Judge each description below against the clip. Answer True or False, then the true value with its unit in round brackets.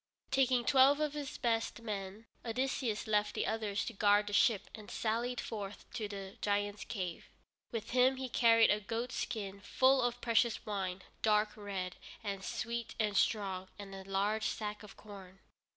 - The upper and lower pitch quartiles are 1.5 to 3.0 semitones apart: True (2.7 semitones)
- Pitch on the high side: True (215 Hz)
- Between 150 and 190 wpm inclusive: True (175 wpm)